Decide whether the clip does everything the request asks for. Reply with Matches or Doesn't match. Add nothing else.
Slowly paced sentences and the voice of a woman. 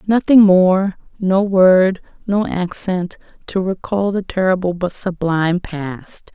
Matches